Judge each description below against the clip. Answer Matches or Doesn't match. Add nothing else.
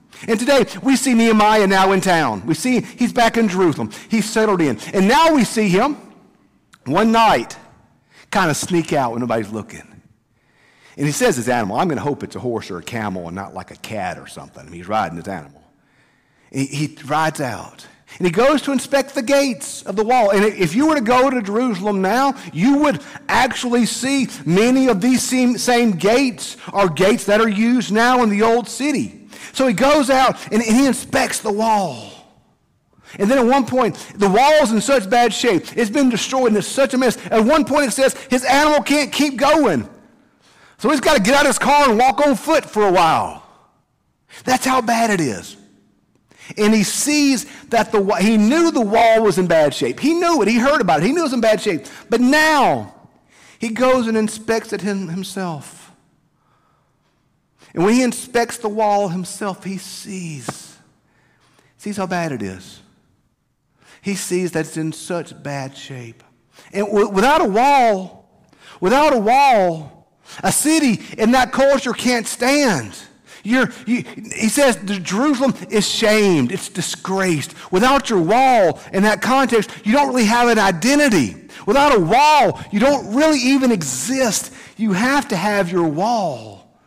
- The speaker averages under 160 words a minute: Doesn't match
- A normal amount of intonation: Doesn't match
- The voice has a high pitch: Matches